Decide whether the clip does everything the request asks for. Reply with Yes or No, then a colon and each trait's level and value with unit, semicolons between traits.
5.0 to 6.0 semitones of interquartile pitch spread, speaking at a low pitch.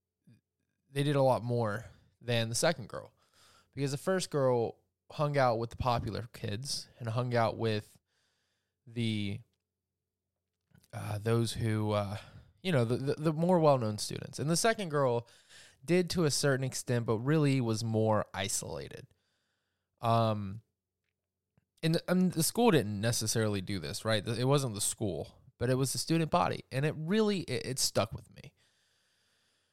Yes: average, 5.3 semitones; low, 115 Hz